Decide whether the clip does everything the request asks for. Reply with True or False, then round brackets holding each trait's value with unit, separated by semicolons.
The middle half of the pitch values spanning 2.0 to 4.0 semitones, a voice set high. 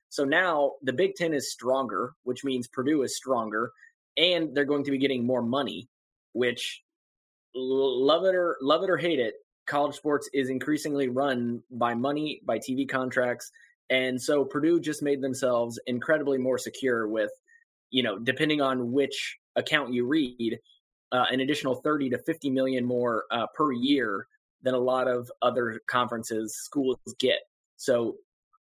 False (3.2 semitones; 135 Hz)